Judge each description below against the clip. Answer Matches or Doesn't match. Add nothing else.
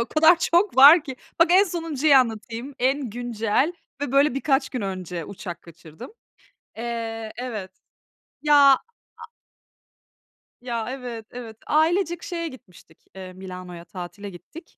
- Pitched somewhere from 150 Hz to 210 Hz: Doesn't match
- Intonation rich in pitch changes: Matches